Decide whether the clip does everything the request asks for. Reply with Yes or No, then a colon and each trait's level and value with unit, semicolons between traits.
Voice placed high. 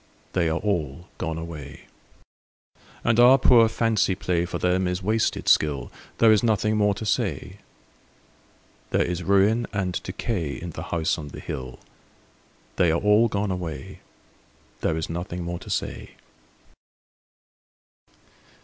No: very low, 90 Hz